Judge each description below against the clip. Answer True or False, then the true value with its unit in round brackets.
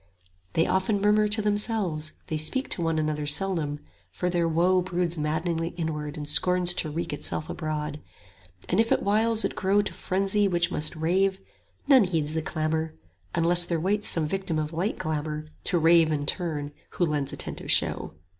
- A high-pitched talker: False (170 Hz)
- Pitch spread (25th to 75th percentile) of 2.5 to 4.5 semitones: True (3.6 semitones)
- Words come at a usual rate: True (180 wpm)